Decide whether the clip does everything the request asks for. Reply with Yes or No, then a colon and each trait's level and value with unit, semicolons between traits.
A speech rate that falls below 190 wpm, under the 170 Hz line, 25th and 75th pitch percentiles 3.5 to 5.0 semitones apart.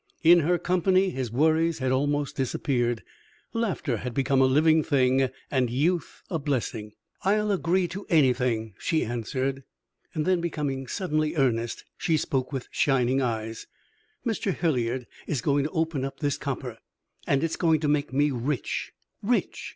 Yes: average, 155 wpm; medium, 140 Hz; average, 4.3 semitones